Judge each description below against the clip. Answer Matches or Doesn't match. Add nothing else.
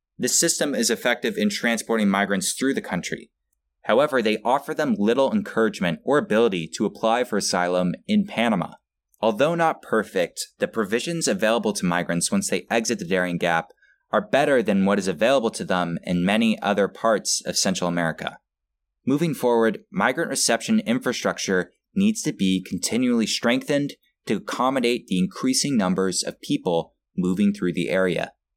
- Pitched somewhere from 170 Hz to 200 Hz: Doesn't match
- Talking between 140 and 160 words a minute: Matches